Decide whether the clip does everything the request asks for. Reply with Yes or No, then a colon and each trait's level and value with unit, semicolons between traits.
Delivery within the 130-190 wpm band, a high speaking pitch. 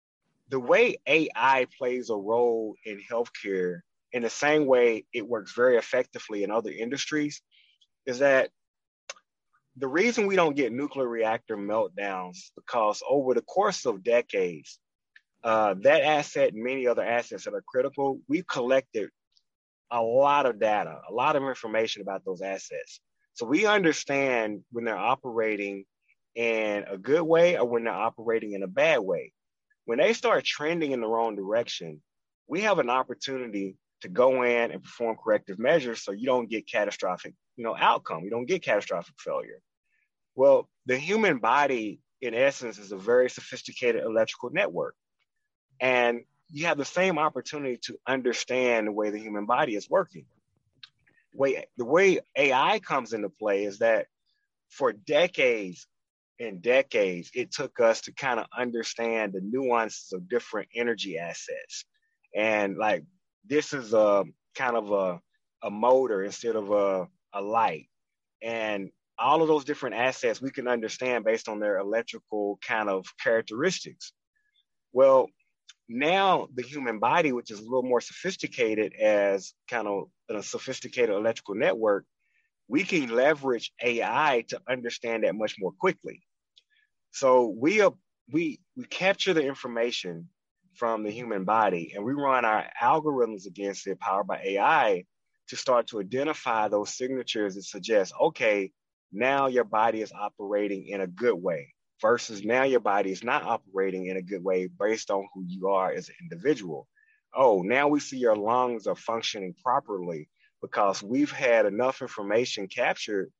No: average, 155 wpm; low, 125 Hz